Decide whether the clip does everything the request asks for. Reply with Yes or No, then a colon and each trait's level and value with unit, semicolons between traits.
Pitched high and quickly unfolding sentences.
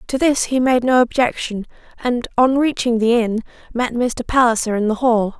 No: high, 240 Hz; average, 190 wpm